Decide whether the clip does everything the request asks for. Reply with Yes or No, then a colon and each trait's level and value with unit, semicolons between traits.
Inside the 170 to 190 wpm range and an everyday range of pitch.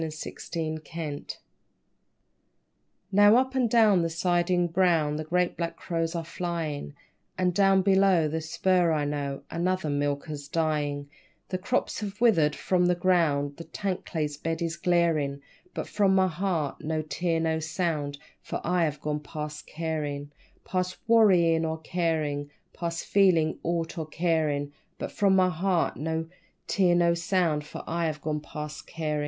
No: average, 155 wpm; average, 3.0 semitones